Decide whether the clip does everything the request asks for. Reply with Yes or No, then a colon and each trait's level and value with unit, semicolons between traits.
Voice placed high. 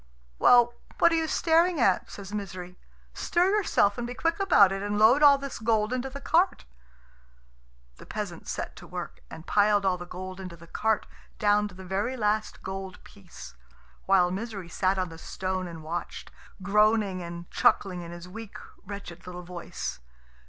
Yes: high, 200 Hz